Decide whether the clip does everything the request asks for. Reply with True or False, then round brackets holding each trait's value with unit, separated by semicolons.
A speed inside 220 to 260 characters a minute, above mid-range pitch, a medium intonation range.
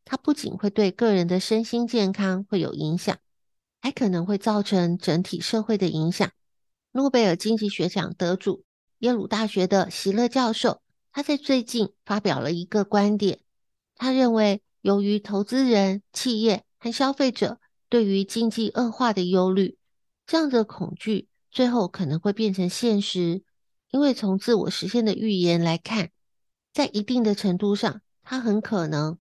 True (240 characters per minute; 205 Hz; 3.7 semitones)